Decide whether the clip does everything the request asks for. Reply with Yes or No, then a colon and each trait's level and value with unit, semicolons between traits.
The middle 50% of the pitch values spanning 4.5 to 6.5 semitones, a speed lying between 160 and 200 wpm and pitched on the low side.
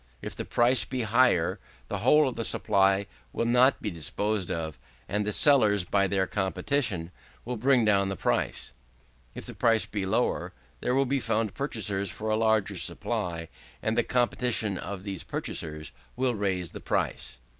No: average, 4.0 semitones; average, 170 wpm; low, 105 Hz